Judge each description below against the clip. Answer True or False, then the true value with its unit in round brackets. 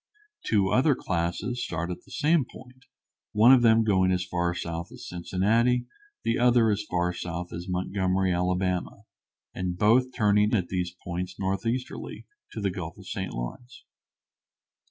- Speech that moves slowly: False (155 wpm)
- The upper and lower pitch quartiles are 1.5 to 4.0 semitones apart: False (4.9 semitones)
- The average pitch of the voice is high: False (95 Hz)